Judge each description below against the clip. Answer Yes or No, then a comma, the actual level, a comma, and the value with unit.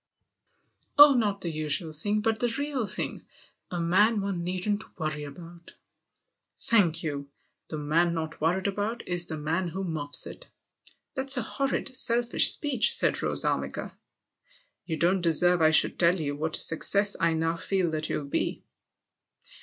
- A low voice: No, medium, 175 Hz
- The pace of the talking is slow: No, average, 170 wpm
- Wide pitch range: No, average, 4.7 semitones